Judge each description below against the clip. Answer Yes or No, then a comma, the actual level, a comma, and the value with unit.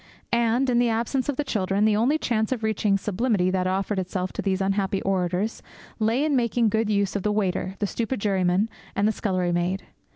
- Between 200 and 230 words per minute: Yes, fast, 205 wpm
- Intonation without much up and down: No, average, 3.3 semitones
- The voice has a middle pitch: No, high, 210 Hz